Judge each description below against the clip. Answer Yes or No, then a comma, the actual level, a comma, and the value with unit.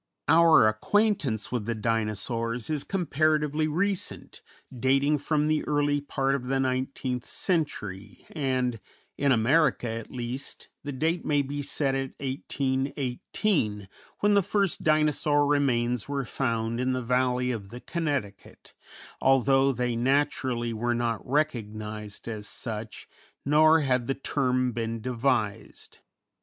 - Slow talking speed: Yes, slow, 125 wpm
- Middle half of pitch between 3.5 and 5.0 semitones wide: Yes, average, 3.8 semitones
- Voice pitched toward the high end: No, low, 130 Hz